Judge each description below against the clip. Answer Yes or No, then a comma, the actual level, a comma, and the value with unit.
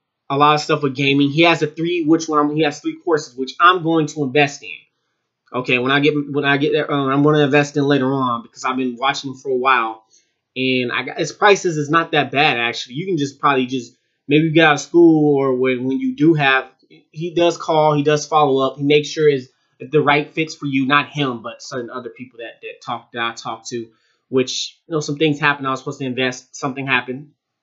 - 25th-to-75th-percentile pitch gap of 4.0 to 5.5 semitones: No, average, 2.7 semitones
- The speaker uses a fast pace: Yes, fast, 250 wpm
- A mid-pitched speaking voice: Yes, medium, 145 Hz